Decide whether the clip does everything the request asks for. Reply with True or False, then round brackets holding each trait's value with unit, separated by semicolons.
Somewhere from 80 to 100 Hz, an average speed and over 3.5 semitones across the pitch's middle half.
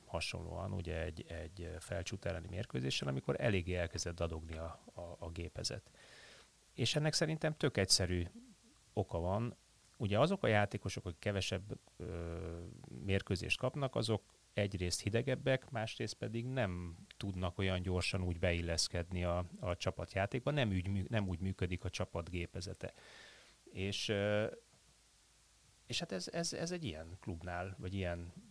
True (95 Hz; 135 wpm; 4.3 semitones)